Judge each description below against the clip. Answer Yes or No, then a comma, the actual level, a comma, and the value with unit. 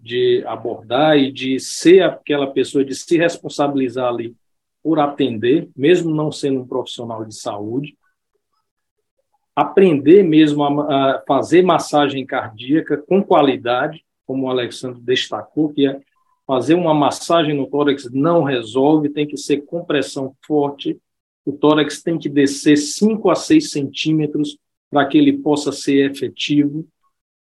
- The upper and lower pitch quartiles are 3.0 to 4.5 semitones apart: Yes, average, 3.7 semitones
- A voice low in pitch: No, medium, 145 Hz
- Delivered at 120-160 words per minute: Yes, slow, 135 wpm